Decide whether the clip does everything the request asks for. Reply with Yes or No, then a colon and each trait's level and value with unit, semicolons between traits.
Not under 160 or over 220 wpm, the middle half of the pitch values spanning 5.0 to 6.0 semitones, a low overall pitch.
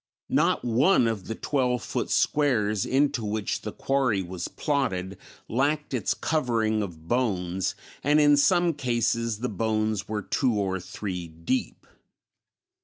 No: slow, 135 wpm; average, 5.3 semitones; low, 115 Hz